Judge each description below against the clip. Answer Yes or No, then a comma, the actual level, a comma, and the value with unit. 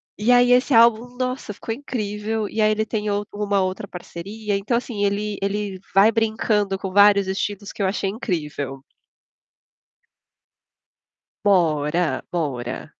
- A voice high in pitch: Yes, high, 205 Hz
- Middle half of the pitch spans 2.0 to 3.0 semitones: Yes, narrow, 2.5 semitones